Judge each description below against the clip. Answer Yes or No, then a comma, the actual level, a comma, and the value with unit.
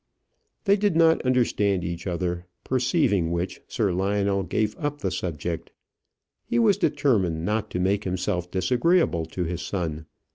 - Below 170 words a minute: Yes, average, 145 wpm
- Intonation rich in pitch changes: Yes, wide, 6.5 semitones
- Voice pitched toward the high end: No, very low, 95 Hz